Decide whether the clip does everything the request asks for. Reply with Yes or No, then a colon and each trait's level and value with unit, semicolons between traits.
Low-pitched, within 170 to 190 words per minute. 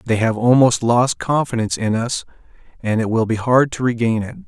No: low, 120 Hz; average, 200 wpm